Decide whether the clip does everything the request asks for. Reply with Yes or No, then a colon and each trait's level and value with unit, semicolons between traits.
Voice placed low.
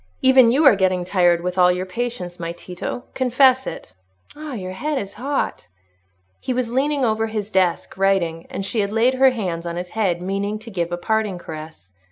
No: high, 200 Hz